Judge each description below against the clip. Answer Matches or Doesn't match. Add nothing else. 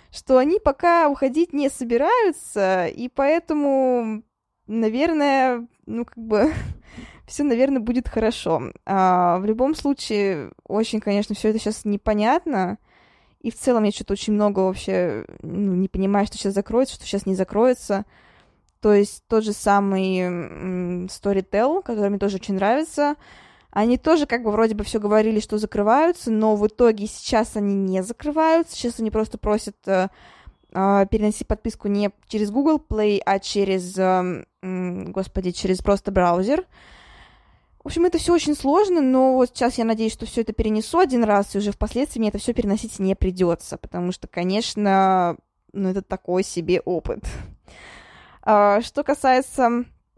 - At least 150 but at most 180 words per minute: Matches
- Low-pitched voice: Doesn't match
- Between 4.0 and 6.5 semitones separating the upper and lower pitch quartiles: Matches